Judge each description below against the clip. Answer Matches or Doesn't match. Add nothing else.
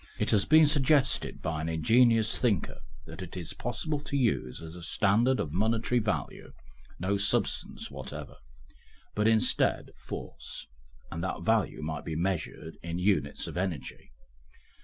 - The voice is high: Doesn't match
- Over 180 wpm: Doesn't match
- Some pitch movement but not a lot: Doesn't match